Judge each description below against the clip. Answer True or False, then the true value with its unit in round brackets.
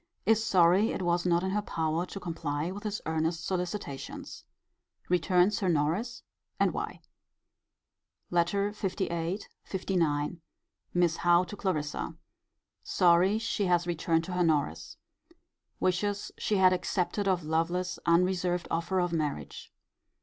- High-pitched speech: False (180 Hz)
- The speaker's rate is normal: False (125 wpm)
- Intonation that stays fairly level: True (2.3 semitones)